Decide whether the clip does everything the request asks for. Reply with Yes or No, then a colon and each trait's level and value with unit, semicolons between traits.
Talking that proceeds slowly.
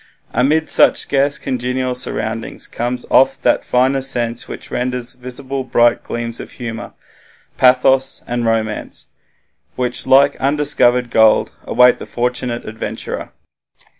Yes: slow, 120 wpm